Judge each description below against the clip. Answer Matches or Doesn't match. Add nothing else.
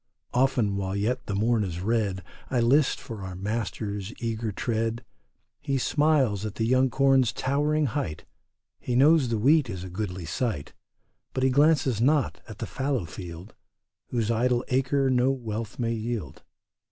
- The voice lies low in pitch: Matches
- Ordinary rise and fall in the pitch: Matches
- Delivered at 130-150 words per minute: Doesn't match